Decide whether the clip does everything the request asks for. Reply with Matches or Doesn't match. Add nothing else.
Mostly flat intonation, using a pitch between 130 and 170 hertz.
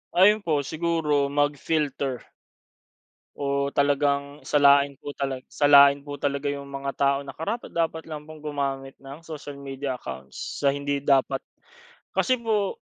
Matches